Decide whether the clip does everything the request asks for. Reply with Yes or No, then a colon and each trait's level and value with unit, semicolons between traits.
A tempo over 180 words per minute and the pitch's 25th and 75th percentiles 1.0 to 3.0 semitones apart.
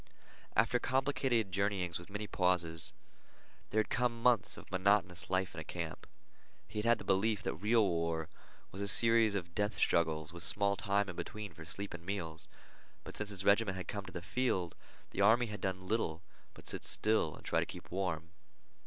No: average, 195 wpm; average, 3.6 semitones